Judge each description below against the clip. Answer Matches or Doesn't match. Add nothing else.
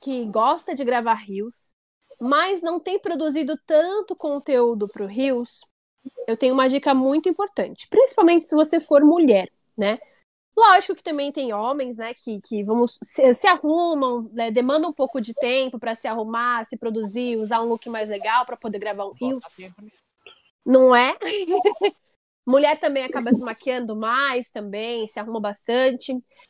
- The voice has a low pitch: Doesn't match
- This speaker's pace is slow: Doesn't match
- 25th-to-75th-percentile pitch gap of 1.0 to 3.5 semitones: Doesn't match